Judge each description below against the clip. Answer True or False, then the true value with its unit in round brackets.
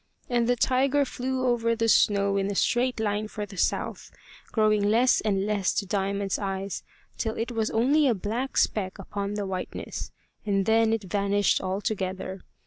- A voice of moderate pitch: False (210 Hz)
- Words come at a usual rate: True (170 wpm)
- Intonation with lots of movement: False (2.7 semitones)